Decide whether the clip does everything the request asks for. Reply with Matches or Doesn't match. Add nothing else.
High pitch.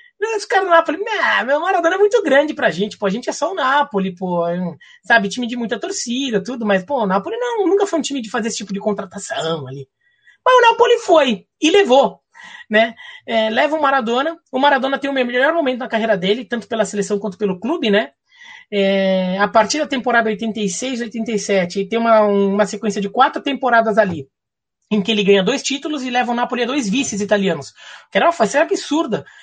Matches